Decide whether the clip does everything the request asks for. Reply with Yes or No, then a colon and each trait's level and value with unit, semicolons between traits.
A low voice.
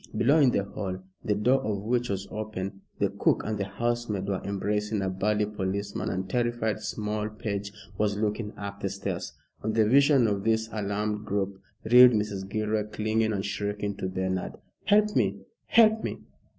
Yes: low, 105 Hz